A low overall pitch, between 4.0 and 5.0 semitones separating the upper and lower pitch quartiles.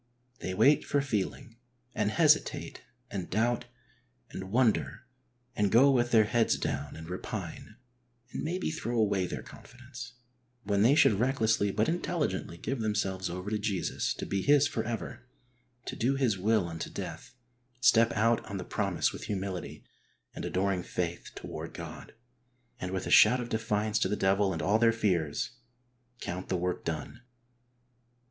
Yes: low, 110 Hz; average, 4.3 semitones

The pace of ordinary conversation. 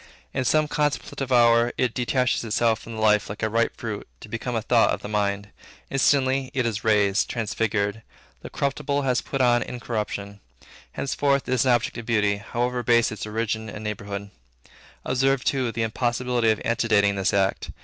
Yes: average, 180 wpm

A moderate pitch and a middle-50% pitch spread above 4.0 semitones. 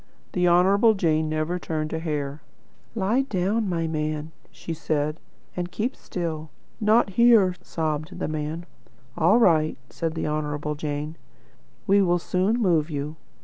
No: medium, 165 Hz; average, 3.6 semitones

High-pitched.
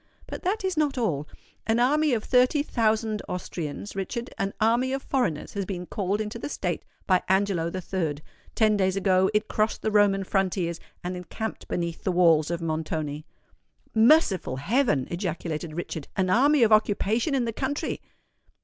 Yes: high, 200 Hz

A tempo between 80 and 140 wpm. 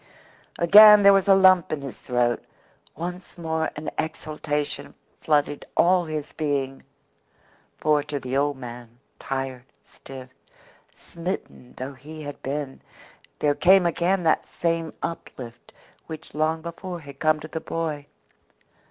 Yes: slow, 135 wpm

